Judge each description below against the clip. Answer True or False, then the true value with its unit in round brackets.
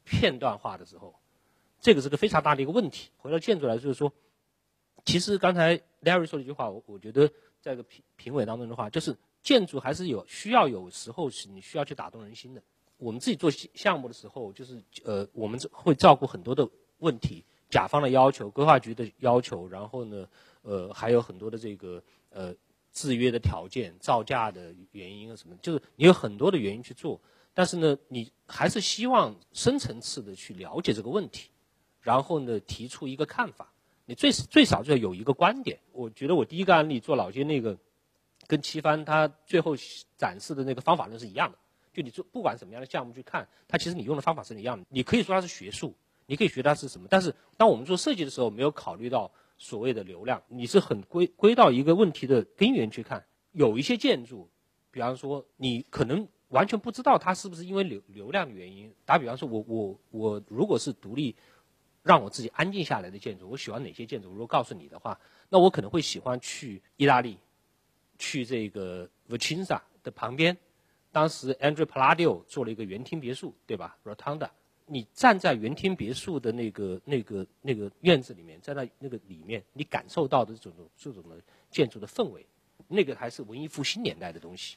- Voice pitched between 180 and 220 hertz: False (135 Hz)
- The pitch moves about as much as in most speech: False (7.1 semitones)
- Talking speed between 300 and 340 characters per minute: True (330 characters per minute)